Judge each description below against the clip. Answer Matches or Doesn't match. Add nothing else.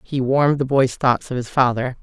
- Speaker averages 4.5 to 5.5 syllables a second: Matches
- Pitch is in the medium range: Doesn't match